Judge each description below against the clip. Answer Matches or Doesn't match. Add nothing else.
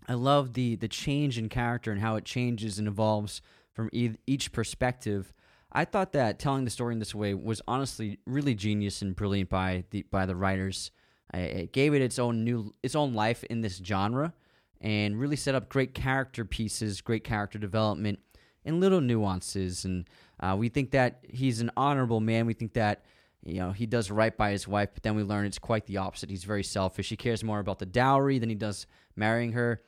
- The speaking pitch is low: Matches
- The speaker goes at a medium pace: Doesn't match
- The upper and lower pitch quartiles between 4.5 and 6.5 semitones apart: Doesn't match